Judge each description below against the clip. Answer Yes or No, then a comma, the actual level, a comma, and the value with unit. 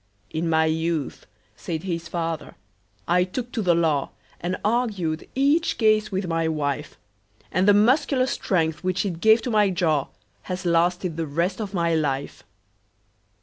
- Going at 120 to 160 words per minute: Yes, average, 155 wpm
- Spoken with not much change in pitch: No, average, 4.2 semitones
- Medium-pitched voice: Yes, medium, 175 Hz